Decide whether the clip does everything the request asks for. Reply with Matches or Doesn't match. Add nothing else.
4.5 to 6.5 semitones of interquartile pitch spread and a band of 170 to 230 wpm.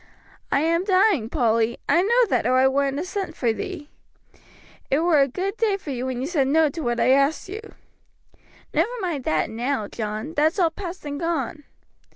Matches